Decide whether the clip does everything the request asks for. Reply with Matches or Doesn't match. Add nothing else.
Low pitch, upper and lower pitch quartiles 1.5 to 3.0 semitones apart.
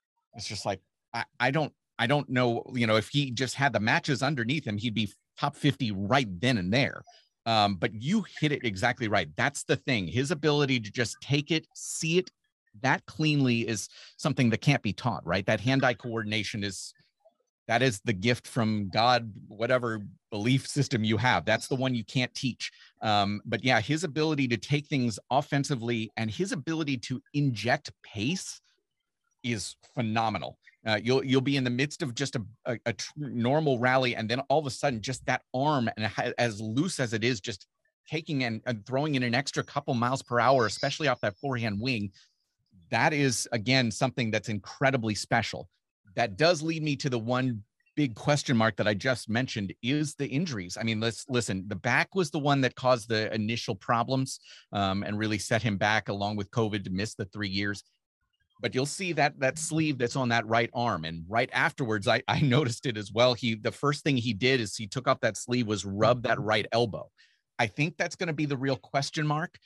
Doesn't match